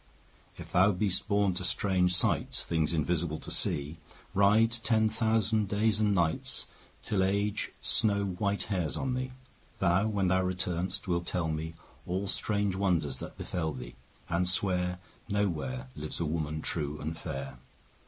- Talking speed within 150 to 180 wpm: Yes, average, 165 wpm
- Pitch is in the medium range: No, very low, 95 Hz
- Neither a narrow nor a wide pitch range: Yes, average, 3.6 semitones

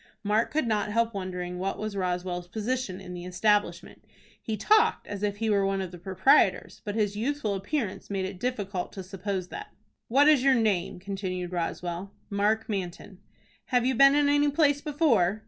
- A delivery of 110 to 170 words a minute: No, average, 180 wpm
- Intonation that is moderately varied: Yes, average, 4.9 semitones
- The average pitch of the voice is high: Yes, high, 205 Hz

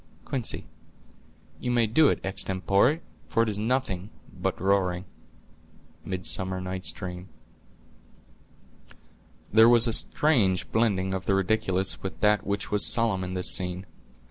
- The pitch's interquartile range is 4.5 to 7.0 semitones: No, average, 3.3 semitones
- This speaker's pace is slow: Yes, slow, 125 wpm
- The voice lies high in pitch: No, low, 100 Hz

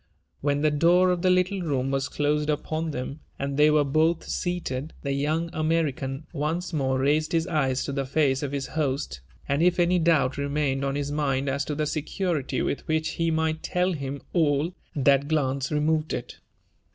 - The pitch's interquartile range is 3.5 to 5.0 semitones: No, narrow, 2.6 semitones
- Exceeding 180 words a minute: Yes, average, 190 wpm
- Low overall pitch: No, medium, 150 Hz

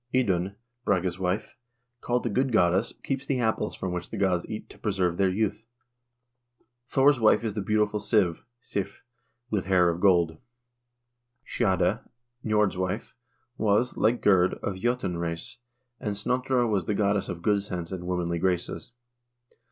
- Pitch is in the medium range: No, low, 100 Hz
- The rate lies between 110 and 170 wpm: Yes, average, 150 wpm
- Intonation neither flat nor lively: Yes, average, 3.6 semitones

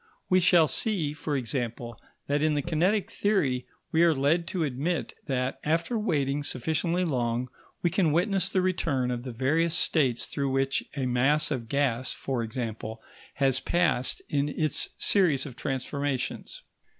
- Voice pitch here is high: No, medium, 145 Hz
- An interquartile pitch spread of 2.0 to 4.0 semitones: No, average, 4.7 semitones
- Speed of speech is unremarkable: Yes, average, 155 wpm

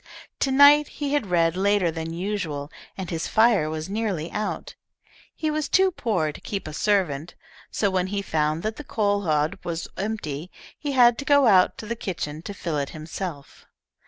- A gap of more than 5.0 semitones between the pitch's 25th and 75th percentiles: Yes, wide, 5.6 semitones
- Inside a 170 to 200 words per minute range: Yes, average, 190 wpm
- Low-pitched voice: No, high, 190 Hz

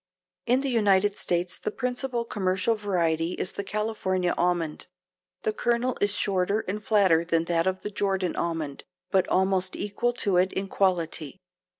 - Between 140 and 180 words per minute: Yes, average, 160 wpm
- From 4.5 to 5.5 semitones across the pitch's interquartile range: No, average, 3.0 semitones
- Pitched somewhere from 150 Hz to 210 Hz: Yes, high, 190 Hz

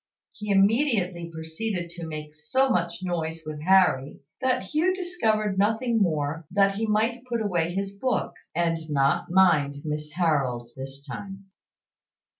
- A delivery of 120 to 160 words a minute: Yes, average, 145 wpm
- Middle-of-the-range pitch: Yes, medium, 180 Hz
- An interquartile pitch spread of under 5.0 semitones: No, wide, 5.6 semitones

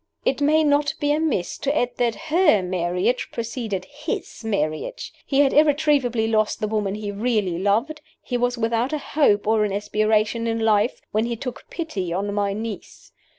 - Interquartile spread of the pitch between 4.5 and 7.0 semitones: Yes, average, 5.3 semitones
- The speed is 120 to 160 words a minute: No, average, 175 wpm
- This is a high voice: Yes, high, 225 Hz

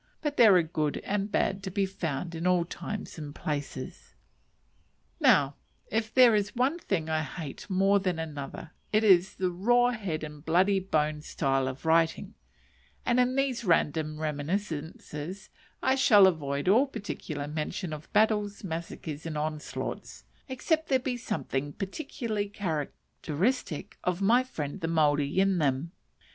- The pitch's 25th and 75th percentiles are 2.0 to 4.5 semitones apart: No, wide, 5.4 semitones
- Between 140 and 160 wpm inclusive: Yes, average, 150 wpm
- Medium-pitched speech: Yes, medium, 180 Hz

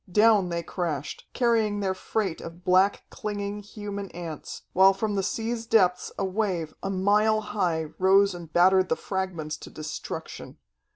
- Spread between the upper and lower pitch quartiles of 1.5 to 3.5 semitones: Yes, average, 2.8 semitones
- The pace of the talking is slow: No, average, 155 wpm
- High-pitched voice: Yes, high, 195 Hz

